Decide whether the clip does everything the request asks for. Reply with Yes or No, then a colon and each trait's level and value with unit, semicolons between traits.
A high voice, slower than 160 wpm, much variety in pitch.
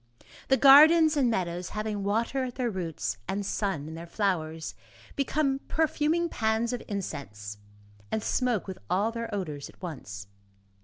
Yes: high, 210 Hz; average, 150 wpm; wide, 7.2 semitones